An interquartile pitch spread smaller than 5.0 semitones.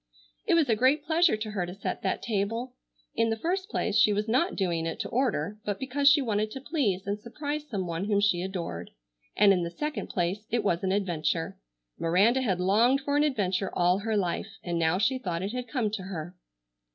No: wide, 5.6 semitones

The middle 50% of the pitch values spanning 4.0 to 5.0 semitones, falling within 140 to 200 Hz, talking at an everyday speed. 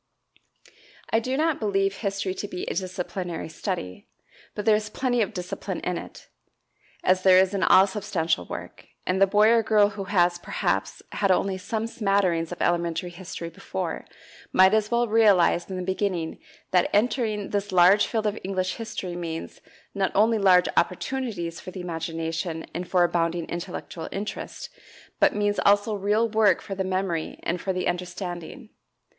No: average, 3.0 semitones; high, 190 Hz; average, 165 wpm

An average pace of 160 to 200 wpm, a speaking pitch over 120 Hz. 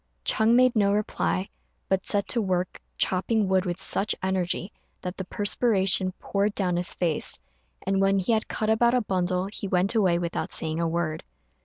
Yes: average, 180 wpm; high, 190 Hz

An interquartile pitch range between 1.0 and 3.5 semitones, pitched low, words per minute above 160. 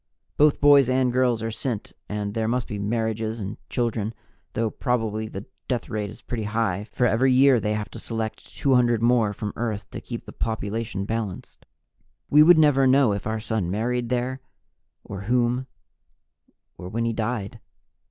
Yes: narrow, 2.6 semitones; low, 115 Hz; average, 170 wpm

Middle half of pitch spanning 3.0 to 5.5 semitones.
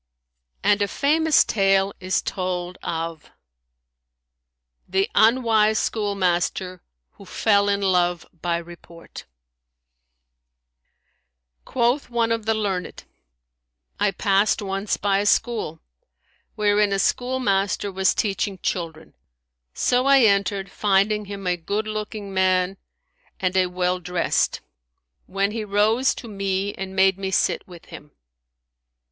No: narrow, 2.5 semitones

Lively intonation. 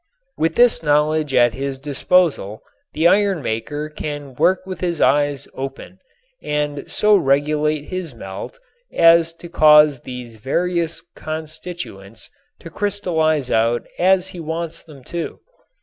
No: average, 3.8 semitones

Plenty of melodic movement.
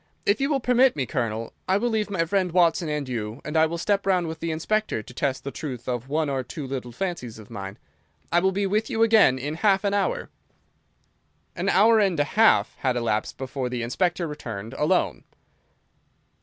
Yes: wide, 7.7 semitones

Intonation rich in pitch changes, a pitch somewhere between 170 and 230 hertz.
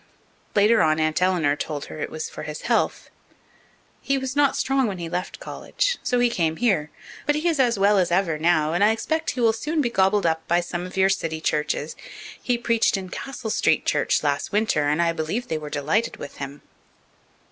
Yes: wide, 7.0 semitones; high, 190 Hz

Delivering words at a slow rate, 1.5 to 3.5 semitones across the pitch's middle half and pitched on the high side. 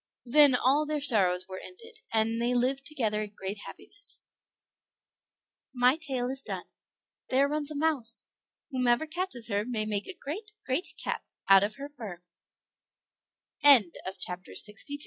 No: slow, 125 wpm; wide, 5.4 semitones; very high, 255 Hz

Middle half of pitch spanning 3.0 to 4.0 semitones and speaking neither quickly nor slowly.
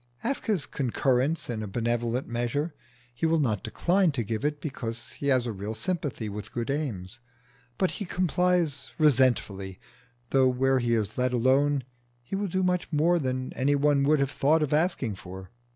No: average, 4.7 semitones; average, 180 wpm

